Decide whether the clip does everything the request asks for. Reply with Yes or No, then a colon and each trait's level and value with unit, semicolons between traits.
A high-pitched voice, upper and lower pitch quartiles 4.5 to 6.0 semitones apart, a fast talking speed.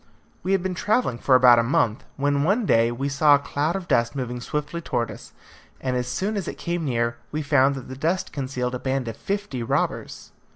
No: medium, 140 Hz; wide, 5.4 semitones; fast, 220 wpm